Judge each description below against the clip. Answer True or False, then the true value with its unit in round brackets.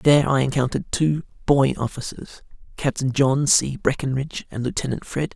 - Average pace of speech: True (145 wpm)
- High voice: False (135 Hz)